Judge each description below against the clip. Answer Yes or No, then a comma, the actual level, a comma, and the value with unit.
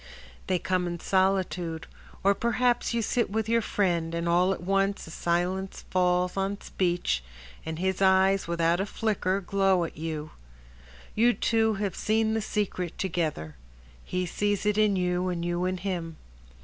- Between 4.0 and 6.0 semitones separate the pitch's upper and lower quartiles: No, narrow, 2.6 semitones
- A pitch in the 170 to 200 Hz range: Yes, medium, 185 Hz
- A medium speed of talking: Yes, average, 160 wpm